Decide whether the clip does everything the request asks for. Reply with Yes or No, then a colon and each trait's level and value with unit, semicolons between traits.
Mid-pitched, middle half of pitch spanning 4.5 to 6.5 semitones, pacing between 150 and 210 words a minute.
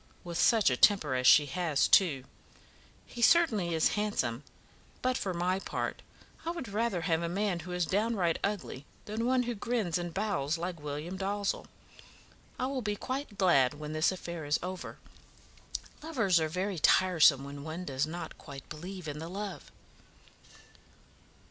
Yes: medium, 180 Hz; average, 5.0 semitones; average, 160 wpm